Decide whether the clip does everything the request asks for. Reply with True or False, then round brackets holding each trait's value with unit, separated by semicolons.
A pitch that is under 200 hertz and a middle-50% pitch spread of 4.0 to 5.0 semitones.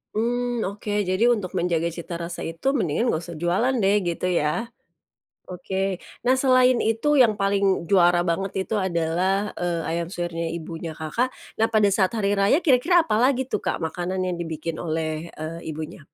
True (185 Hz; 4.6 semitones)